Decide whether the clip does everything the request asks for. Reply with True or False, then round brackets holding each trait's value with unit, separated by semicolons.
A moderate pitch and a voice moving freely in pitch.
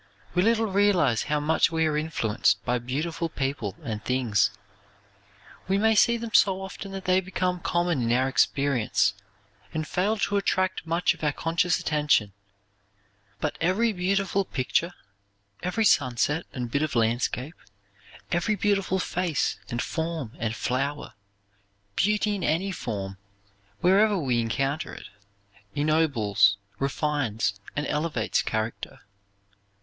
True (155 Hz; 6.7 semitones)